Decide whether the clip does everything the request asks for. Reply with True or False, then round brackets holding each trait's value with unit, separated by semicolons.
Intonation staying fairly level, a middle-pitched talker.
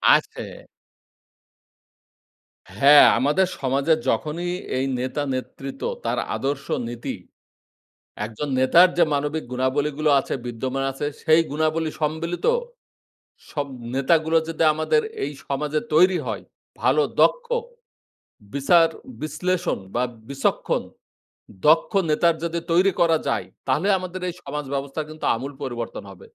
False (3.4 semitones; 150 Hz)